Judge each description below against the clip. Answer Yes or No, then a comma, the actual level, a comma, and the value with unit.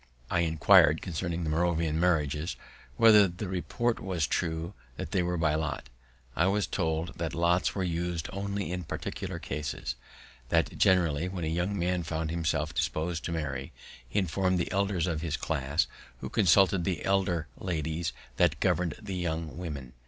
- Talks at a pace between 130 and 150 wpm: No, average, 165 wpm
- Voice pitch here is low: Yes, very low, 85 Hz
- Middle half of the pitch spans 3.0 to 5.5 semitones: No, narrow, 2.4 semitones